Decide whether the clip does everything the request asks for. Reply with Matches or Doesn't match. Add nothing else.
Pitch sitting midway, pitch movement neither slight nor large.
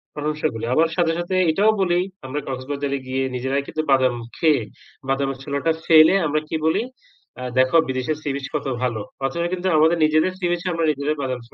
Matches